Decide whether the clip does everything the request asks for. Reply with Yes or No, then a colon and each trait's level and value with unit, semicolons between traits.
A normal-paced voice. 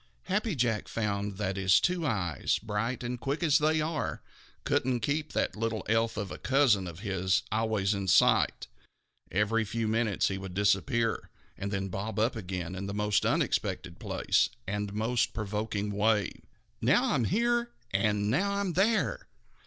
Yes: average, 160 wpm